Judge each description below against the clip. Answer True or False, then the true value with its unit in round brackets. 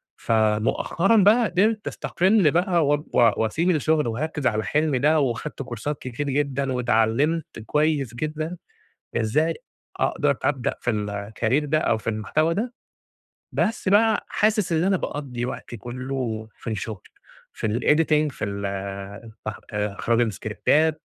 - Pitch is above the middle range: False (140 Hz)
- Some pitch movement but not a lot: False (6.1 semitones)